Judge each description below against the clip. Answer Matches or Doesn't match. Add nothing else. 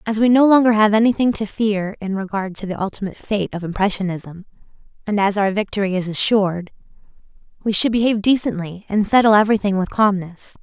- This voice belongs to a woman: Matches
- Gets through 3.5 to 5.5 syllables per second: Doesn't match